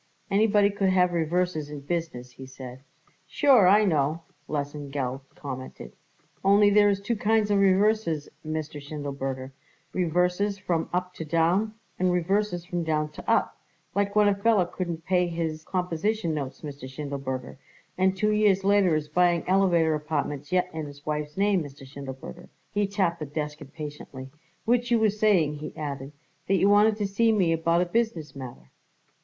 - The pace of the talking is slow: No, average, 165 wpm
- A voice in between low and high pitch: Yes, medium, 170 Hz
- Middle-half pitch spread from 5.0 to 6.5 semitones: Yes, average, 5.3 semitones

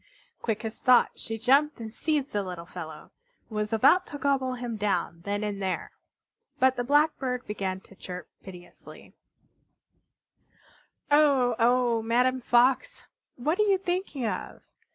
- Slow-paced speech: No, average, 145 wpm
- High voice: Yes, high, 240 Hz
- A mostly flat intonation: No, average, 4.5 semitones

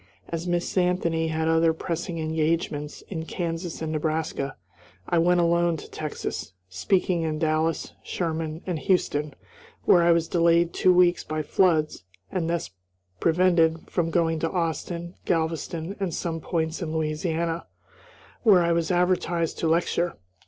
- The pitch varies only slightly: Yes, narrow, 1.4 semitones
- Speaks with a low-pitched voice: No, medium, 165 Hz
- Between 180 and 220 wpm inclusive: No, average, 145 wpm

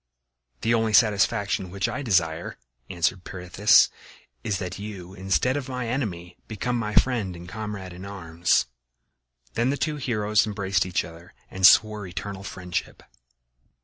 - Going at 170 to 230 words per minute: No, average, 145 wpm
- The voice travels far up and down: No, average, 3.6 semitones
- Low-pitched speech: Yes, low, 100 Hz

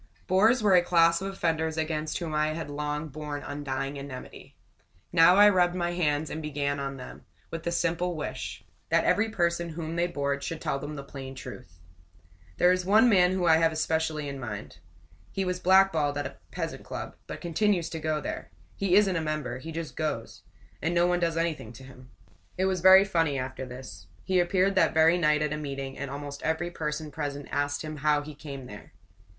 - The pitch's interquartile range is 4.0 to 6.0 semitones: No, average, 3.5 semitones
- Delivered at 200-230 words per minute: Yes, fast, 205 wpm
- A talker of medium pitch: Yes, medium, 160 Hz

